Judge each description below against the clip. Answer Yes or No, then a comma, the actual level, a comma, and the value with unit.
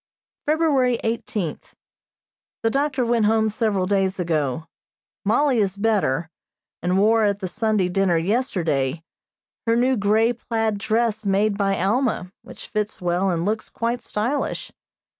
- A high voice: Yes, high, 210 Hz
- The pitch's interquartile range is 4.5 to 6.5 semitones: No, average, 3.6 semitones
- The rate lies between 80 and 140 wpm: Yes, slow, 135 wpm